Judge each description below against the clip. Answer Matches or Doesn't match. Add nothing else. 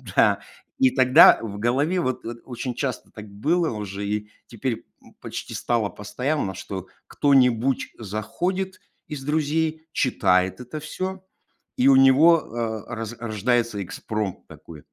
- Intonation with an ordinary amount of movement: Doesn't match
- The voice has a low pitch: Matches